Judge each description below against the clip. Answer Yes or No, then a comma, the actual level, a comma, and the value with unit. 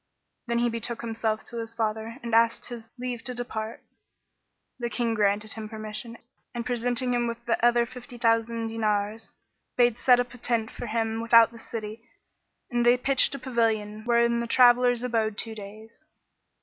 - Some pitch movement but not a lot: No, narrow, 1.5 semitones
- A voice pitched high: Yes, high, 230 Hz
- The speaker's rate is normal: Yes, average, 170 wpm